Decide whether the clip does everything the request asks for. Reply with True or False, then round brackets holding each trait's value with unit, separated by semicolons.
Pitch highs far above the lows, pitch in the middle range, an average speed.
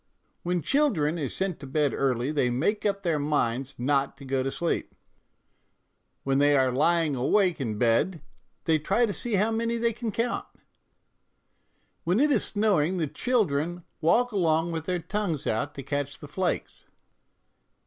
True (6.1 semitones; 160 Hz; 170 wpm)